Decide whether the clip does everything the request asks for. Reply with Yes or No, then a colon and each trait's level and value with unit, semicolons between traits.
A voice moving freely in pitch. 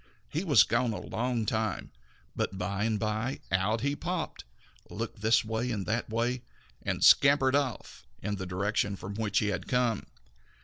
No: average, 3.4 semitones